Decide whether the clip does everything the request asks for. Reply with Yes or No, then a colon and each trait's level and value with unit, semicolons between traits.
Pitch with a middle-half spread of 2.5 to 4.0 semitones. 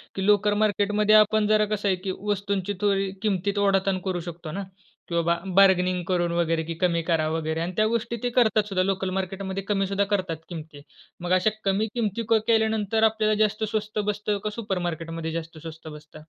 Yes: average, 3.5 semitones